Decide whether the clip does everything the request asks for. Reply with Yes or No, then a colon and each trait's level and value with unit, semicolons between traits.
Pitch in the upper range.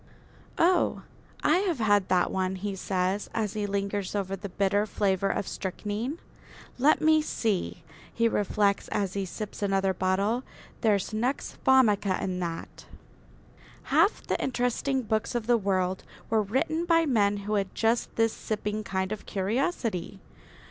Yes: high, 205 Hz